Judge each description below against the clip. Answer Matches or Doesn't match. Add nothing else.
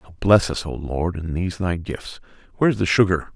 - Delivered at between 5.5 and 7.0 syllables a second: Matches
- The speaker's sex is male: Matches